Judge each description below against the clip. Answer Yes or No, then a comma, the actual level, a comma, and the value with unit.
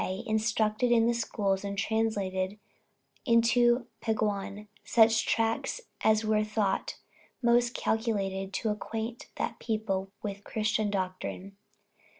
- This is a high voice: Yes, high, 215 Hz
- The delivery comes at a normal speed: No, slow, 110 wpm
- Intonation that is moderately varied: No, narrow, 2.2 semitones